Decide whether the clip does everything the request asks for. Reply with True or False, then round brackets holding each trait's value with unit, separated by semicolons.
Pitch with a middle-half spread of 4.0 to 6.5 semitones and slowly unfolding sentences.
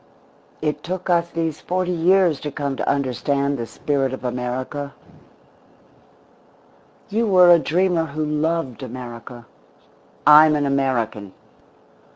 True (4.5 semitones; 120 wpm)